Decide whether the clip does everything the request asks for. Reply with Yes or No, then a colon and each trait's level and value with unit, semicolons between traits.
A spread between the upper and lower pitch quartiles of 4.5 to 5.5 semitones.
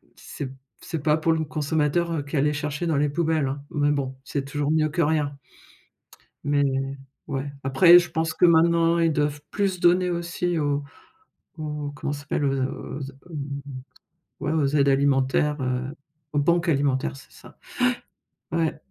No: narrow, 2.6 semitones